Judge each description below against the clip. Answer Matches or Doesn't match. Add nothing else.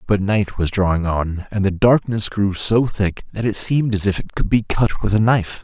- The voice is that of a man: Matches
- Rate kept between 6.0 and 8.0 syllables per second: Doesn't match